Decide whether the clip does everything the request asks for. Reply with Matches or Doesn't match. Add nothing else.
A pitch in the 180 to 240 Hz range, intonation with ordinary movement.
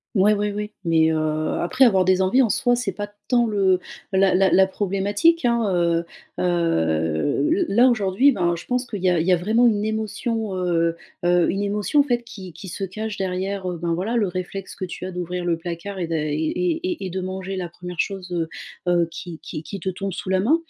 Matches